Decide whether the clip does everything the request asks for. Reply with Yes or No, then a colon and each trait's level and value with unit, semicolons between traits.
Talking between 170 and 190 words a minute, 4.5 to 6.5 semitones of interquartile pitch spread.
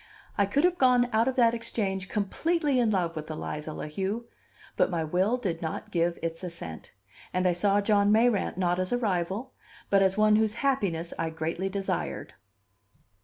Yes: average, 180 wpm; average, 5.0 semitones